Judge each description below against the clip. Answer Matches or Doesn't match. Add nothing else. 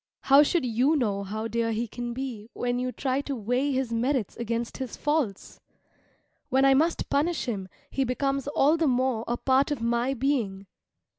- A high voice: Matches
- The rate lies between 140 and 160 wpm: Doesn't match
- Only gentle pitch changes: Doesn't match